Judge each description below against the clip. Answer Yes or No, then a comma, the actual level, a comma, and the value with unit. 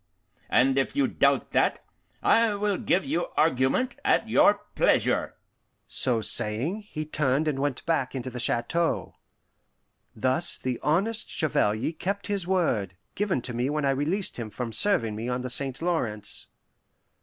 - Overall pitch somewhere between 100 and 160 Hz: Yes, medium, 140 Hz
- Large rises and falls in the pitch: Yes, wide, 6.2 semitones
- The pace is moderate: Yes, average, 155 wpm